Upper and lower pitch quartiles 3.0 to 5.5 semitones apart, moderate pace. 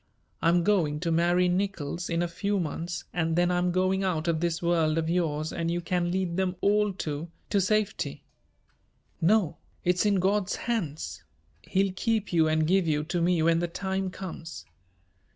No: narrow, 2.5 semitones; average, 175 wpm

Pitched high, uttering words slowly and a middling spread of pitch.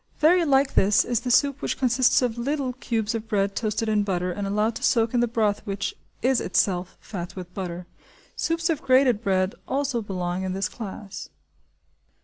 No: high, 220 Hz; average, 185 wpm; average, 4.7 semitones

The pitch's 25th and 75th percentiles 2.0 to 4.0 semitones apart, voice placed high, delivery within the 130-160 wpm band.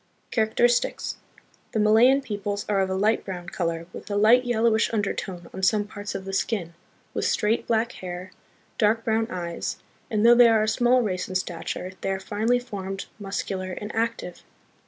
No: average, 3.1 semitones; high, 210 Hz; average, 175 wpm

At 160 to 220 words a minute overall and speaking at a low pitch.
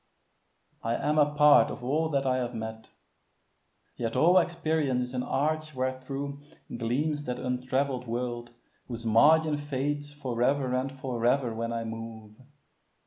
No: average, 145 wpm; low, 130 Hz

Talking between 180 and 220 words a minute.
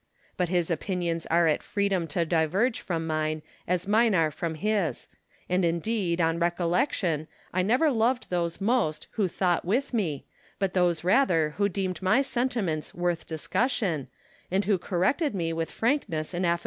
No: average, 160 wpm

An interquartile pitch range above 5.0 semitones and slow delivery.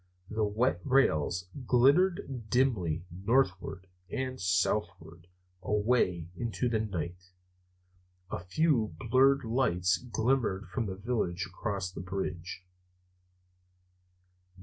Yes: wide, 5.6 semitones; slow, 95 wpm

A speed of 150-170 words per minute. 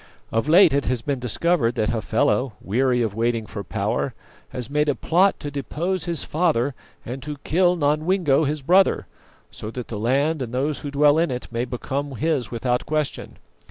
No: average, 185 wpm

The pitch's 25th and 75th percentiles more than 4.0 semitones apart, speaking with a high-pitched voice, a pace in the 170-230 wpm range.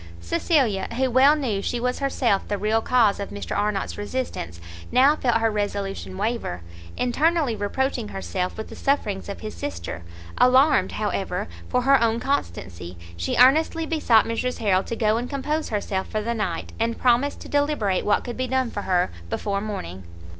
Yes: average, 4.7 semitones; high, 230 Hz; average, 175 wpm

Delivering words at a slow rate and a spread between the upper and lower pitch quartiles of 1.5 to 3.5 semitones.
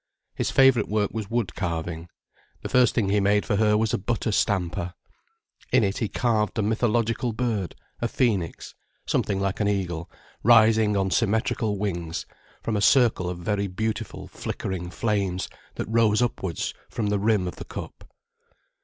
No: average, 160 wpm; average, 2.9 semitones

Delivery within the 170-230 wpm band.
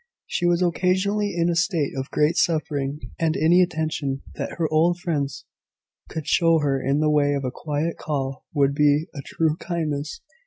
Yes: average, 180 wpm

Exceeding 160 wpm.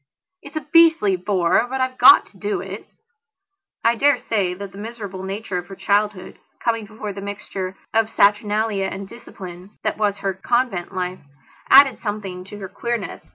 Yes: average, 170 wpm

